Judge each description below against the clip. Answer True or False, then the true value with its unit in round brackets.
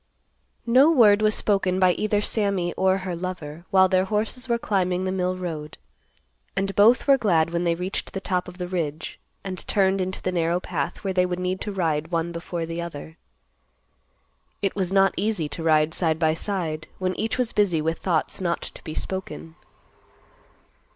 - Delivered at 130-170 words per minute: False (185 wpm)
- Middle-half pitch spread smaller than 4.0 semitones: True (2.7 semitones)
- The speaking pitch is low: False (185 Hz)